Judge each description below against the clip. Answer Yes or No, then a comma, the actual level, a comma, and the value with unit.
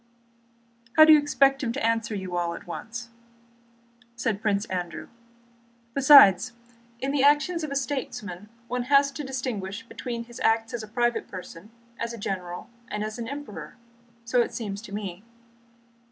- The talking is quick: No, average, 165 wpm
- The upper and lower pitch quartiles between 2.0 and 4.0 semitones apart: No, average, 4.9 semitones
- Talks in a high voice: Yes, high, 230 Hz